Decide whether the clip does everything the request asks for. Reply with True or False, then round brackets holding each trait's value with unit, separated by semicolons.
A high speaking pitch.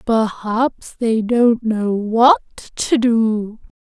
True (225 Hz)